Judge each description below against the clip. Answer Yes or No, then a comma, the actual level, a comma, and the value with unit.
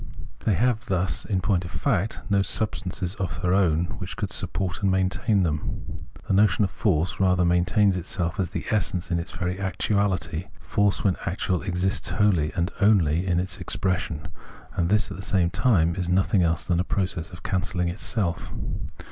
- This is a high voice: No, very low, 95 Hz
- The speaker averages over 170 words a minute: Yes, average, 180 wpm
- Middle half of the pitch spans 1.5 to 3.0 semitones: Yes, narrow, 2.4 semitones